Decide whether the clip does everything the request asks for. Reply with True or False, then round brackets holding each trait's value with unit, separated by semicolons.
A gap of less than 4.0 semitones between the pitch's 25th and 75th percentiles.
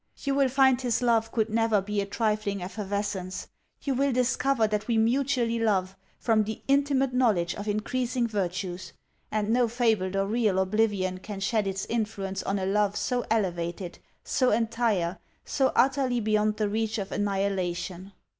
True (3.5 semitones)